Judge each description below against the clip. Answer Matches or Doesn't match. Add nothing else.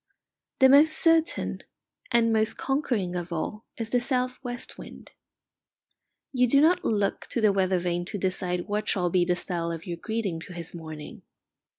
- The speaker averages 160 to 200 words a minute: Matches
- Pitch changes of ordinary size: Doesn't match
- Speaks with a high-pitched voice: Matches